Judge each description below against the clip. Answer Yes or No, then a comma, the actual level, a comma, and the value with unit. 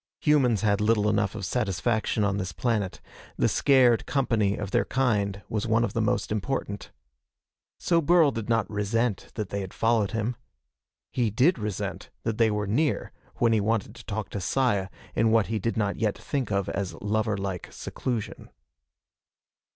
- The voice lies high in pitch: No, low, 110 Hz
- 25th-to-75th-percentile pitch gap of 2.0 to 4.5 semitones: Yes, average, 2.8 semitones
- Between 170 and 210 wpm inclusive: Yes, average, 175 wpm